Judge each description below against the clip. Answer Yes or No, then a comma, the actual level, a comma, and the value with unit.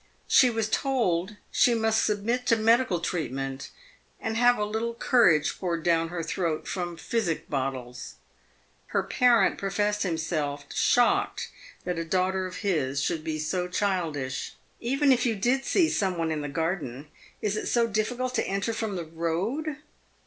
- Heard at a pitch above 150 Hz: Yes, high, 190 Hz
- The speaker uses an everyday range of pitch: No, wide, 5.9 semitones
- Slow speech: No, average, 165 wpm